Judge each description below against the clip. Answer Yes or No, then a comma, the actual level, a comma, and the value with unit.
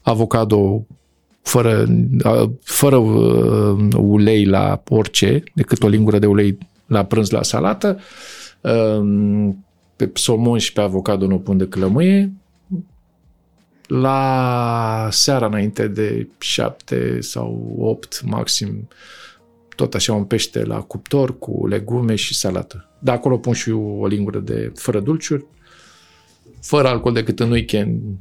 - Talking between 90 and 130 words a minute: Yes, average, 120 wpm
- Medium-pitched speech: No, low, 110 Hz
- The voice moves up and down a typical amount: Yes, average, 3.6 semitones